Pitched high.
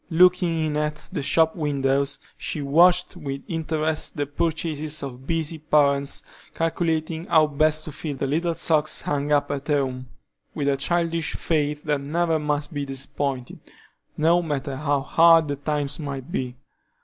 No: medium, 150 Hz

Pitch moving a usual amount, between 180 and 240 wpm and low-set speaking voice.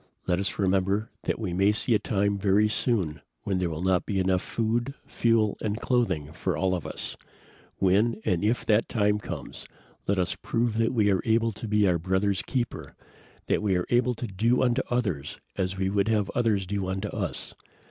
Yes: average, 3.3 semitones; average, 200 wpm; low, 100 Hz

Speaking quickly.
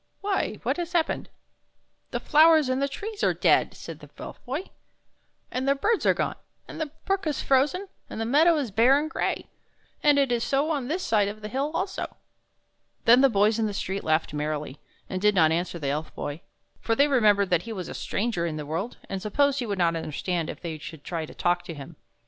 Yes: fast, 235 wpm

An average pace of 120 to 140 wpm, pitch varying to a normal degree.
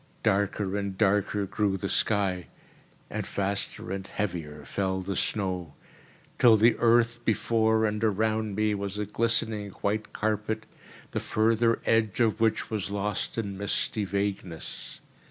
No: slow, 135 wpm; narrow, 2.2 semitones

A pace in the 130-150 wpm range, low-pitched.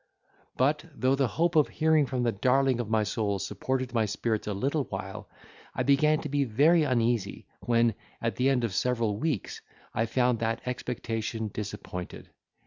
No: average, 170 wpm; low, 120 Hz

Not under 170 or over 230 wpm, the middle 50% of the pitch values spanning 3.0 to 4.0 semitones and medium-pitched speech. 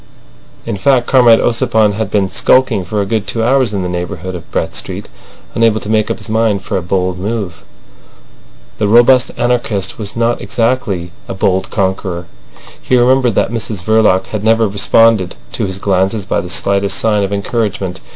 No: average, 180 wpm; average, 3.3 semitones; low, 105 Hz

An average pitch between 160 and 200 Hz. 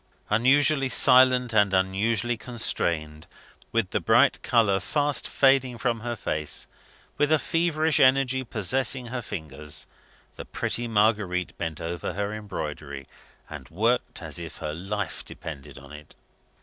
No: low, 110 Hz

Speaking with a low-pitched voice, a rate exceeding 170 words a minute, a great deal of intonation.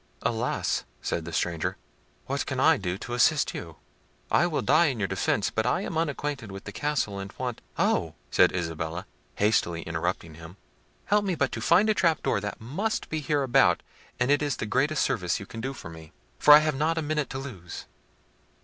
Yes: low, 120 Hz; average, 200 wpm; wide, 8.8 semitones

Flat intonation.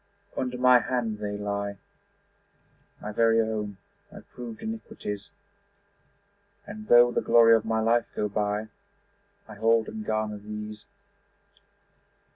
Yes: narrow, 2.3 semitones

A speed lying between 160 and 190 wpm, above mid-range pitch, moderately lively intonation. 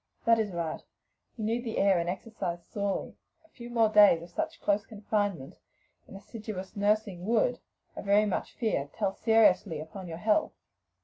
Yes: average, 170 wpm; high, 205 Hz; average, 3.5 semitones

